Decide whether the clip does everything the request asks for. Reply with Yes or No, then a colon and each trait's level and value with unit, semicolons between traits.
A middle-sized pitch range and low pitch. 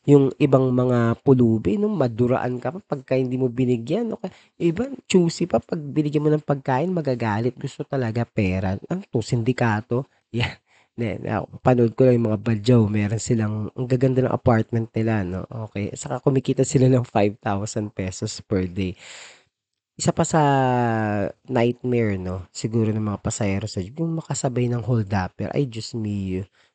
Yes: average, 4.2 semitones; low, 125 Hz